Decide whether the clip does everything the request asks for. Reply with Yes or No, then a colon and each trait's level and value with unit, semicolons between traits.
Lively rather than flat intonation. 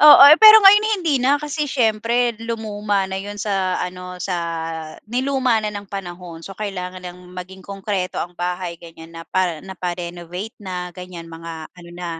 No: average, 3.8 semitones